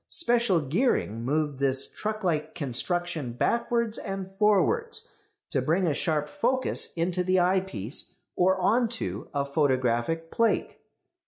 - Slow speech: Yes, slow, 130 wpm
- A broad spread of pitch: Yes, wide, 7.0 semitones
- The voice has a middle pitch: Yes, medium, 175 Hz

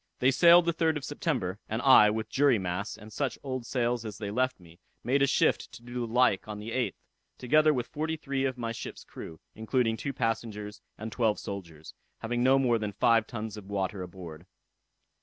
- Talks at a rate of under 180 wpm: No, fast, 205 wpm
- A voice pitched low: Yes, low, 115 Hz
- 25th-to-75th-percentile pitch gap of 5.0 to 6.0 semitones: No, average, 3.9 semitones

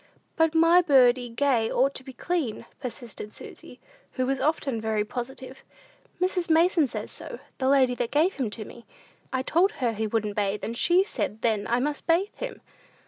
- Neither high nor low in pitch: No, very high, 260 Hz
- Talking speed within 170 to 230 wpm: Yes, average, 185 wpm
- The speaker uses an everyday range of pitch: No, wide, 5.8 semitones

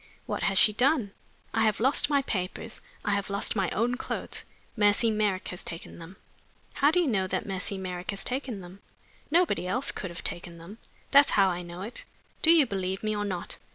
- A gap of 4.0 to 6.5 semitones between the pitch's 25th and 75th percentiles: Yes, average, 4.7 semitones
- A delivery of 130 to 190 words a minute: No, fast, 205 wpm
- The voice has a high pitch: Yes, high, 200 Hz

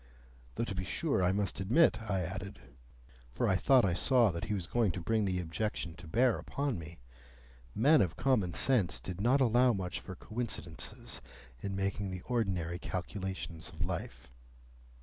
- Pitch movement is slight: No, average, 4.7 semitones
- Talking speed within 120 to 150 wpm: No, average, 170 wpm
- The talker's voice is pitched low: Yes, very low, 95 Hz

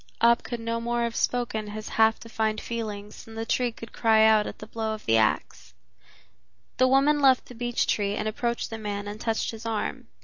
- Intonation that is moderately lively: No, narrow, 1.7 semitones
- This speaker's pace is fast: Yes, fast, 210 wpm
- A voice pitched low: No, high, 225 Hz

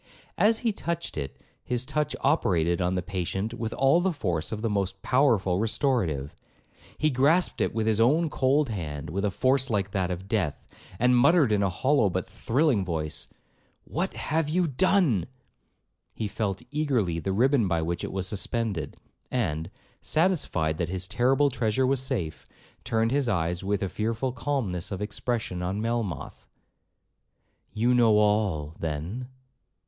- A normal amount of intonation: No, wide, 6.4 semitones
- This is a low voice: Yes, low, 110 Hz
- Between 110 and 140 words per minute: No, average, 160 wpm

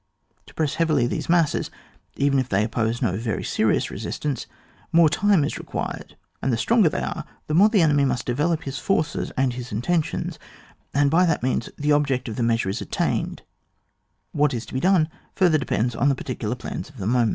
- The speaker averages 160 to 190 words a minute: No, fast, 205 wpm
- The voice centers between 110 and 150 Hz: Yes, medium, 140 Hz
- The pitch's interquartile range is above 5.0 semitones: No, average, 4.6 semitones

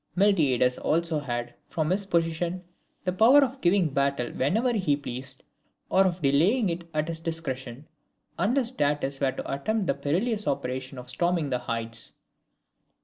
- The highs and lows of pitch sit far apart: Yes, wide, 5.7 semitones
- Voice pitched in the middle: Yes, medium, 160 Hz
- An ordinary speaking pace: Yes, average, 150 wpm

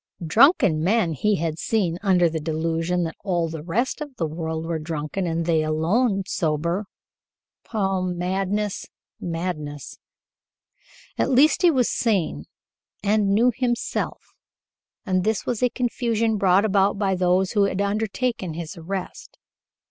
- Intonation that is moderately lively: Yes, average, 4.5 semitones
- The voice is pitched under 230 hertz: Yes, medium, 185 Hz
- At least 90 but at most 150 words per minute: Yes, average, 140 wpm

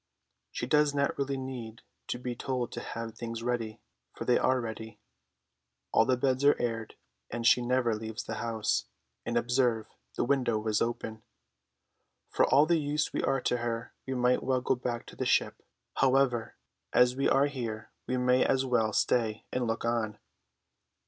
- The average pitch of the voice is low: Yes, low, 120 Hz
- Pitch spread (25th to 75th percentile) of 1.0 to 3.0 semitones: Yes, narrow, 2.4 semitones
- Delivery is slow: No, average, 175 wpm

